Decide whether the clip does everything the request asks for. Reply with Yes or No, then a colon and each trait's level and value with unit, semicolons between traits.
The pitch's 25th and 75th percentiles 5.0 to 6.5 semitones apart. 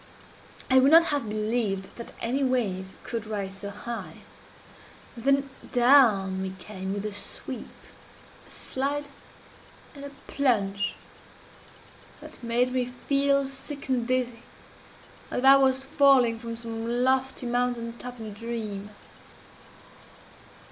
No: average, 3.8 semitones